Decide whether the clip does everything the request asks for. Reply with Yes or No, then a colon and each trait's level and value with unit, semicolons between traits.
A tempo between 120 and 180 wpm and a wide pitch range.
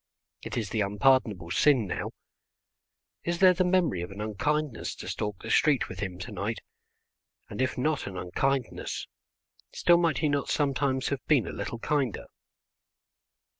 Yes: average, 160 wpm; wide, 6.4 semitones